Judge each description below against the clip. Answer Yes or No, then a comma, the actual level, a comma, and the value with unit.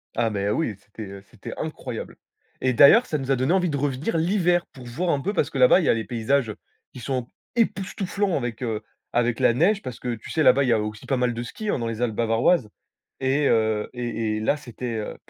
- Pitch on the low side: Yes, low, 125 Hz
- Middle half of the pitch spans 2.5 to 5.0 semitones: No, wide, 5.5 semitones